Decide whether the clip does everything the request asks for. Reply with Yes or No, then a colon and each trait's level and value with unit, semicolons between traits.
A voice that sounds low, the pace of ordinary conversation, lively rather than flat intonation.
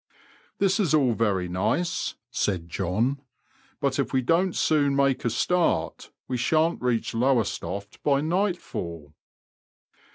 No: low, 130 Hz; slow, 125 wpm; wide, 8.0 semitones